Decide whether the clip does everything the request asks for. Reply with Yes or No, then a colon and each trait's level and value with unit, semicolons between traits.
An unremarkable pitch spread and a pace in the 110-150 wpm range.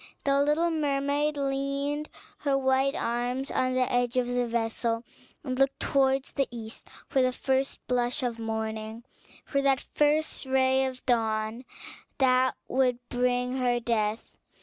No: narrow, 2.3 semitones; average, 145 wpm